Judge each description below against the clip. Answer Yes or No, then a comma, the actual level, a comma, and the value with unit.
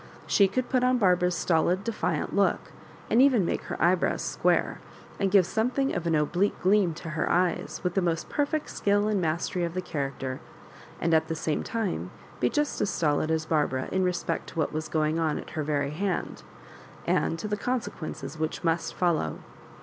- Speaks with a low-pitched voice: No, medium, 175 Hz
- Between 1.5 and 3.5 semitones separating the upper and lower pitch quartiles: No, average, 4.4 semitones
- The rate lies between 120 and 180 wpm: No, average, 195 wpm